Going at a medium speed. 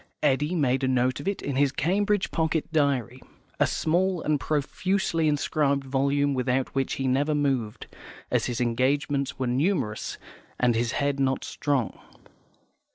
Yes: average, 150 wpm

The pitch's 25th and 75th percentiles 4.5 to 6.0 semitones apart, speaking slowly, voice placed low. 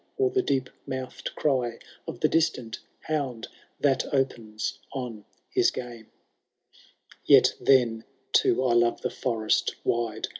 No: average, 2.8 semitones; slow, 125 wpm; low, 125 Hz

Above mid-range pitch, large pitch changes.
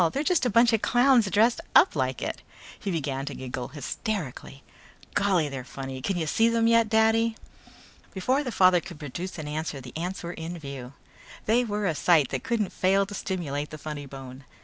No: medium, 175 Hz; wide, 7.7 semitones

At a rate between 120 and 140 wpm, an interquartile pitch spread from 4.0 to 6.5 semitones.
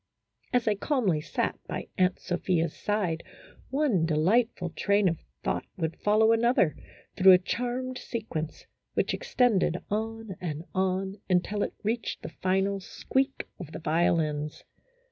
Yes: slow, 135 wpm; average, 4.8 semitones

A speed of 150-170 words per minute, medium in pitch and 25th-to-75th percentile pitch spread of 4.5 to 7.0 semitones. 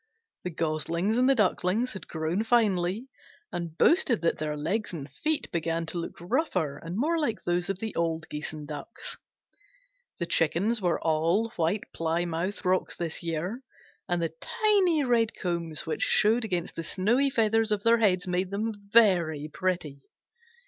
Yes: average, 165 wpm; medium, 180 Hz; average, 5.3 semitones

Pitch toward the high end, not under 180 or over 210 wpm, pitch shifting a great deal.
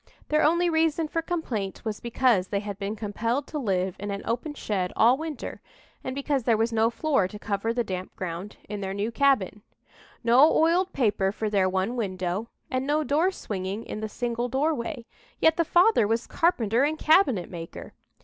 Yes: high, 230 Hz; average, 190 wpm; wide, 6.5 semitones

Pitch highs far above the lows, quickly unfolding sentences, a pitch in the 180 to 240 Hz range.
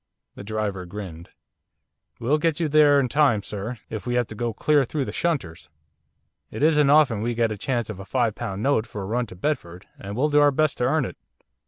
No: wide, 6.0 semitones; fast, 225 wpm; low, 120 Hz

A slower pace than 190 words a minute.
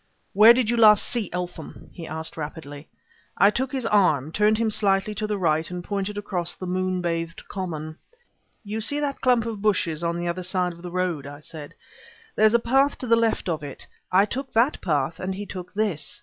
No: fast, 205 wpm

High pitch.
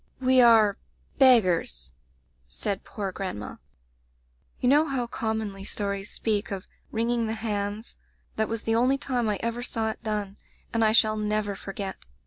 Yes: high, 220 Hz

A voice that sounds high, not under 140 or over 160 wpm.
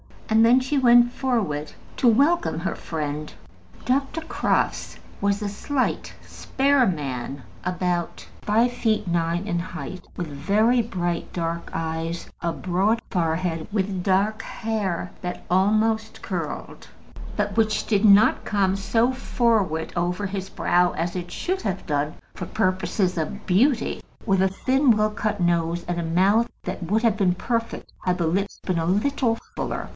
Yes: high, 195 Hz; average, 150 wpm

